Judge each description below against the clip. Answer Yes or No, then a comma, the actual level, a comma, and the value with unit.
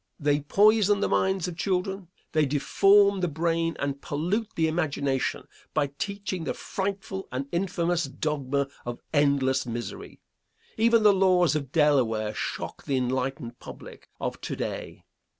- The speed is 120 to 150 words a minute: Yes, average, 140 wpm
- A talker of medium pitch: Yes, medium, 160 Hz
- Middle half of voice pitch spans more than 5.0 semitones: Yes, wide, 5.6 semitones